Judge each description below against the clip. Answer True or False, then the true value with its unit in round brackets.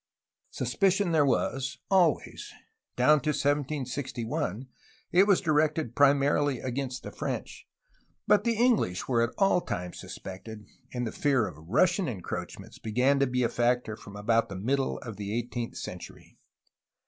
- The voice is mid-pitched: False (130 Hz)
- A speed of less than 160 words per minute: True (145 wpm)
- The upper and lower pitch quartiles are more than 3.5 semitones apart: True (4.6 semitones)